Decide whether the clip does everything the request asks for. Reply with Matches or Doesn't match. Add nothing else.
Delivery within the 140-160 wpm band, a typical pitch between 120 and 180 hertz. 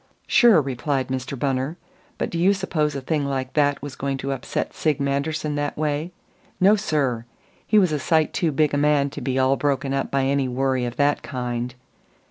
Doesn't match